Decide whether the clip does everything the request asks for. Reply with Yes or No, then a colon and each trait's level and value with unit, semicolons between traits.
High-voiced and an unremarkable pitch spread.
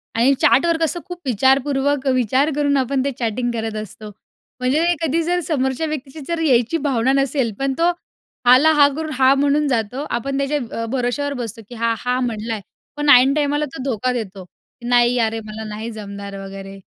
Yes: very high, 260 Hz; average, 3.8 semitones